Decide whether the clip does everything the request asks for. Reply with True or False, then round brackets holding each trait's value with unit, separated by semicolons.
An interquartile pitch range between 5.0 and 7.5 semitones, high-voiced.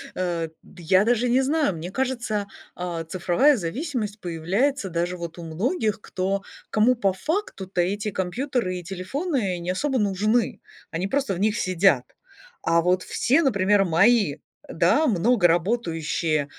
True (5.5 semitones; 195 Hz)